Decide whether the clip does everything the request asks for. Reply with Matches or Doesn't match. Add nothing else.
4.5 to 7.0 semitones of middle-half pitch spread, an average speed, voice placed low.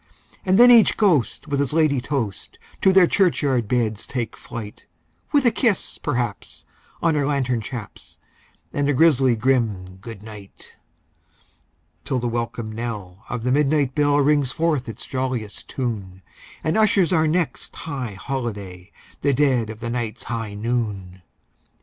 Matches